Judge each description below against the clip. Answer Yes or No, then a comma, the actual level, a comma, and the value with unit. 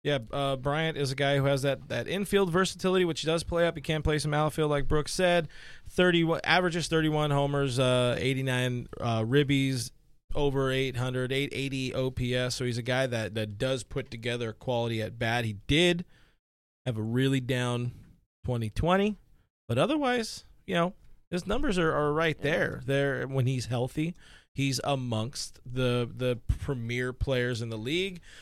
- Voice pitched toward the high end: No, low, 135 Hz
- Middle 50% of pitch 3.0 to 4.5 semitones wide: Yes, average, 4.0 semitones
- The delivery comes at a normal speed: Yes, average, 165 wpm